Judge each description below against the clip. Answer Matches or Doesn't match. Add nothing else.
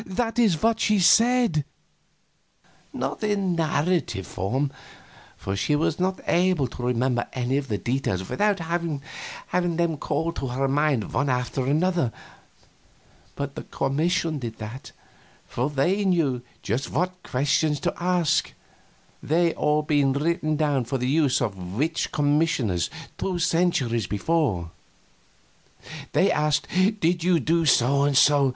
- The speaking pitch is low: Doesn't match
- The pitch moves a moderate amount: Matches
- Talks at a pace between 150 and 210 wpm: Doesn't match